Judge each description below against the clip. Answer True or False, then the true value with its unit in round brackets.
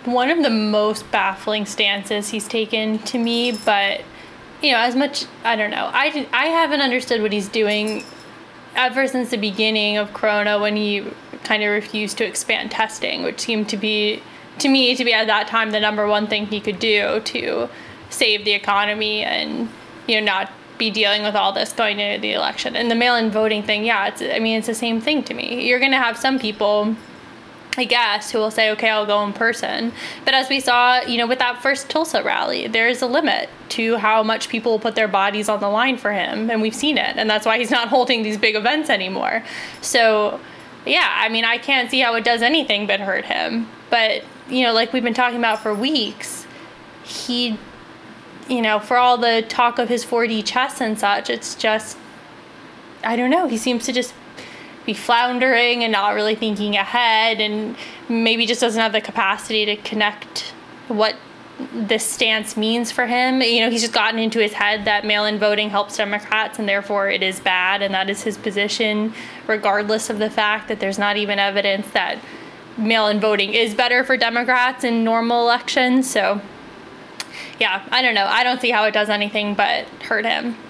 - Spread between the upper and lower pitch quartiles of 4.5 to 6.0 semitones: False (2.7 semitones)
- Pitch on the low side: False (225 Hz)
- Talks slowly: False (205 wpm)